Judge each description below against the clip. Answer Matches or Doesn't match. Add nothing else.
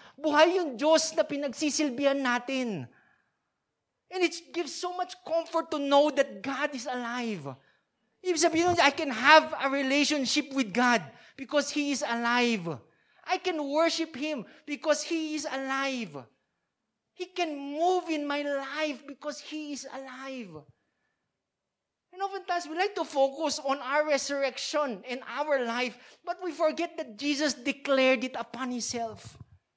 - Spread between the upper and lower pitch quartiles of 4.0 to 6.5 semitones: Doesn't match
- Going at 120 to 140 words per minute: Matches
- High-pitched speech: Matches